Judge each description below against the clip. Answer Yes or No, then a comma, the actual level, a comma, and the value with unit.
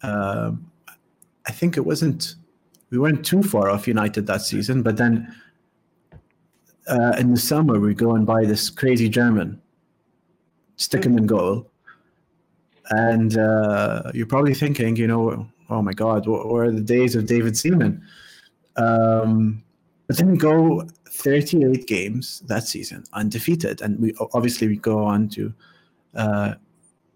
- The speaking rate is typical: Yes, average, 145 wpm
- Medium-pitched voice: No, low, 120 Hz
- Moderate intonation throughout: No, wide, 5.7 semitones